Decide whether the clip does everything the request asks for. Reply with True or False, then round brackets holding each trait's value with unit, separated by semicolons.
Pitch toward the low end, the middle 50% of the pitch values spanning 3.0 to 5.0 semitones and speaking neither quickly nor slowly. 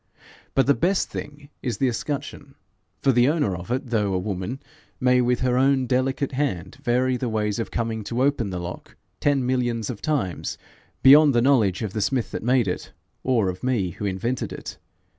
True (125 Hz; 4.1 semitones; 195 wpm)